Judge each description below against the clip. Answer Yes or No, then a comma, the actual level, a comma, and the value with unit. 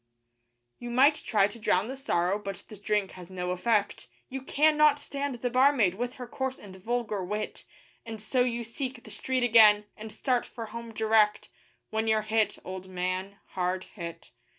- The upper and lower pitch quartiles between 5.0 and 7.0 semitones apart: No, average, 4.0 semitones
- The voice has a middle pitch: No, high, 220 Hz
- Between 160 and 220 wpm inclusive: Yes, average, 175 wpm